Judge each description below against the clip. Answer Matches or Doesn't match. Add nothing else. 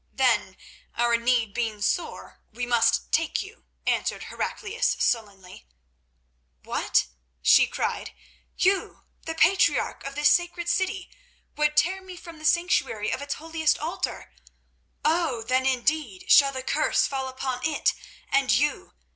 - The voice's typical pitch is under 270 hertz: Doesn't match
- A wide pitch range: Matches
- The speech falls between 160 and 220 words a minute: Doesn't match